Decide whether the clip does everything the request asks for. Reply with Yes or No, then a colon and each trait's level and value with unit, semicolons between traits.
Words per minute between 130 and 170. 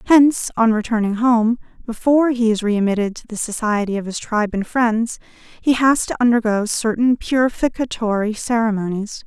Yes: average, 150 wpm